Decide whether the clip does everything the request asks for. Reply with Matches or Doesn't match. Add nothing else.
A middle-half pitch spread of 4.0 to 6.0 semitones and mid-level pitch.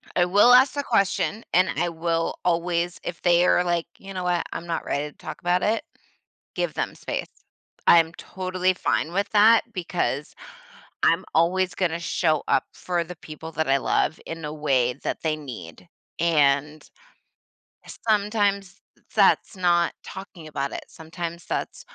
Doesn't match